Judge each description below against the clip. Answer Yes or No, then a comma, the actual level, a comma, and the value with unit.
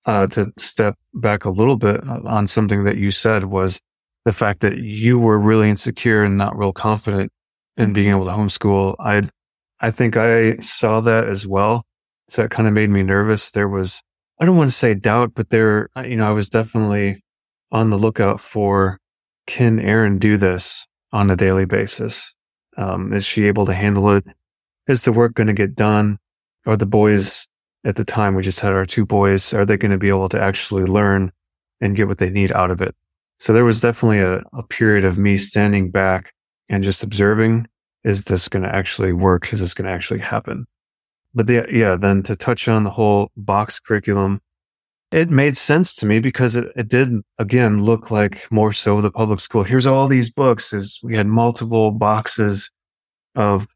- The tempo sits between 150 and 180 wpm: No, average, 200 wpm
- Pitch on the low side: Yes, low, 105 Hz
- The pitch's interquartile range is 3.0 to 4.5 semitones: No, narrow, 2.4 semitones